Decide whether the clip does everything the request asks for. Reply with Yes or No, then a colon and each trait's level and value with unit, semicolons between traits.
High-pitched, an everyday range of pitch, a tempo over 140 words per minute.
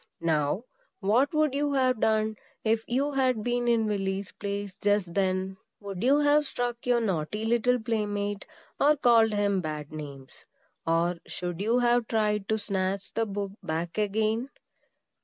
Yes: high, 215 Hz; average, 3.8 semitones; average, 155 wpm